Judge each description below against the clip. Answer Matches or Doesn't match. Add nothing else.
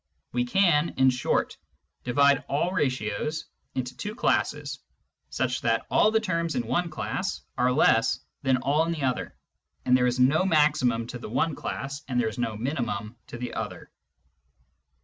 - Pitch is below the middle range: Matches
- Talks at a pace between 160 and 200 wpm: Matches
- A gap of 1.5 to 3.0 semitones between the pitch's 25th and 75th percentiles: Doesn't match